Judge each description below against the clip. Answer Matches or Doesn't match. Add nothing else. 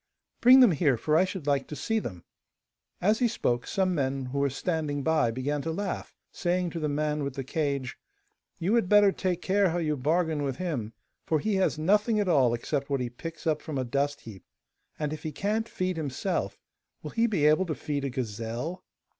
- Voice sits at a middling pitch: Matches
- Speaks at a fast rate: Matches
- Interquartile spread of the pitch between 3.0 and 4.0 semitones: Doesn't match